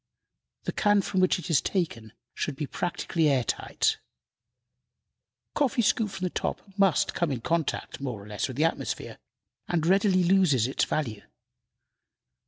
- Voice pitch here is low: No, medium, 165 Hz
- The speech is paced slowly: No, average, 155 wpm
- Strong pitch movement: Yes, wide, 6.1 semitones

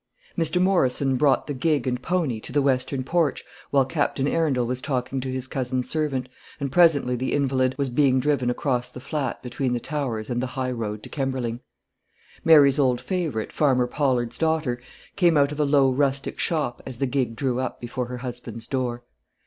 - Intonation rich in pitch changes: No, average, 2.7 semitones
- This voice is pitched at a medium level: No, low, 130 Hz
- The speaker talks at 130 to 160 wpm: No, average, 190 wpm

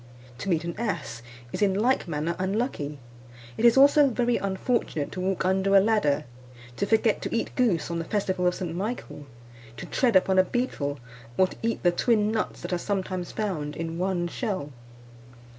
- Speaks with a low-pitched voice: No, high, 190 Hz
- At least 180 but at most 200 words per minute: Yes, average, 185 wpm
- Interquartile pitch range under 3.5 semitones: No, average, 4.5 semitones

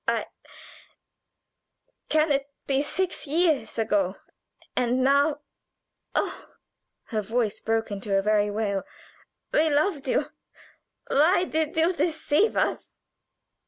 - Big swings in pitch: Yes, wide, 6.3 semitones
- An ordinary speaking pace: No, slow, 110 wpm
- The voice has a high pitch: Yes, very high, 275 Hz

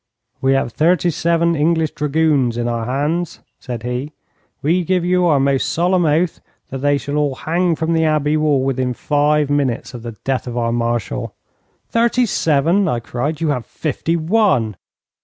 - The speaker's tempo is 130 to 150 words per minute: No, average, 175 wpm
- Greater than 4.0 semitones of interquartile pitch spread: Yes, average, 4.5 semitones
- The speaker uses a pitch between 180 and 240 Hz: No, medium, 150 Hz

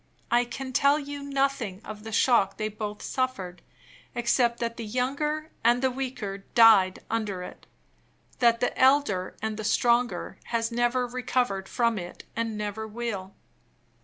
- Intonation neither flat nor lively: Yes, average, 3.3 semitones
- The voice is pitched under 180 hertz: No, high, 235 Hz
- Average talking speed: Yes, average, 150 wpm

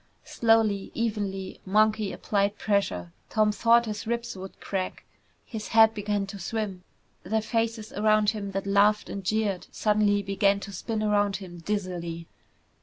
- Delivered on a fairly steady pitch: Yes, narrow, 1.7 semitones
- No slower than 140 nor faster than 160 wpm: Yes, average, 145 wpm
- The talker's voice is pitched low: No, high, 205 Hz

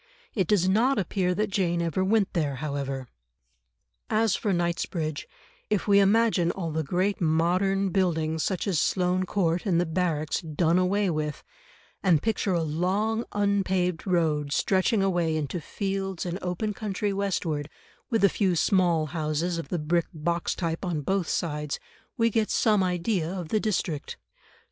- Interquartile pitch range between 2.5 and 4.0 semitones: Yes, average, 3.5 semitones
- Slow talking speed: No, average, 160 wpm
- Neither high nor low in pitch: Yes, medium, 180 Hz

